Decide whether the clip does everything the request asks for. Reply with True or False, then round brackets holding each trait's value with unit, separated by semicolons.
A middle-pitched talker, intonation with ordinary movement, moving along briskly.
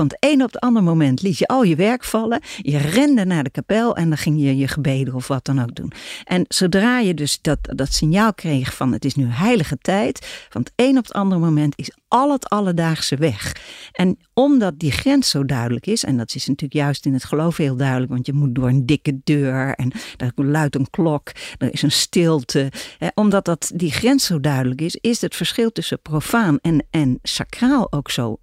False (155 Hz; 6.7 semitones; 215 wpm)